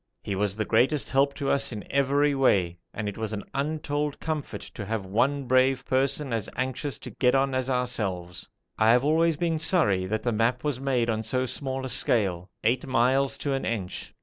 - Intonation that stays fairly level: No, average, 4.1 semitones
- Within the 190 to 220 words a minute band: Yes, average, 200 wpm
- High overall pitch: No, low, 130 Hz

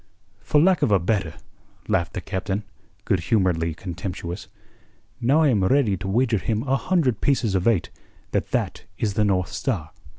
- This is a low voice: Yes, low, 100 Hz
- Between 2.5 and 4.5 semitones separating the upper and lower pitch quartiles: No, wide, 5.5 semitones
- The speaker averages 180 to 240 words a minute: No, average, 170 wpm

